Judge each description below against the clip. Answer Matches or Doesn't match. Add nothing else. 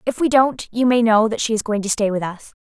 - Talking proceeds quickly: Matches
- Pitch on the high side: Matches